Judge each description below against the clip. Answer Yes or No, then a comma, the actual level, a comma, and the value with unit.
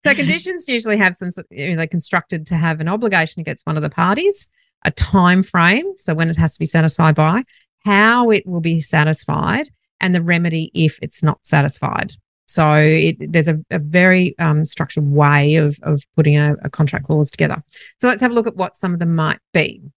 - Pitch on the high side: No, medium, 165 Hz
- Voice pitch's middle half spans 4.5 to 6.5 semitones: No, average, 3.6 semitones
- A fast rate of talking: Yes, fast, 210 wpm